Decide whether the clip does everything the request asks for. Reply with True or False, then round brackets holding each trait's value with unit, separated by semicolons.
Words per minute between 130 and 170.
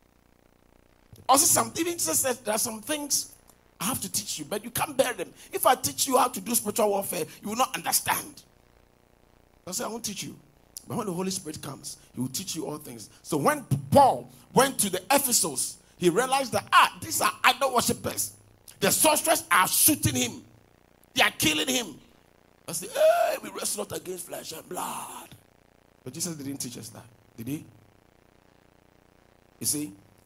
False (180 wpm)